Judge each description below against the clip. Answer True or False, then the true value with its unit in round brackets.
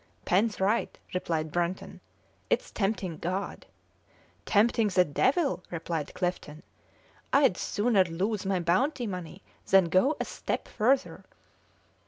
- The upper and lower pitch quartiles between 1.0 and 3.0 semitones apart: False (4.2 semitones)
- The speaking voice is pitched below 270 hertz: True (190 Hz)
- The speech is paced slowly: True (115 wpm)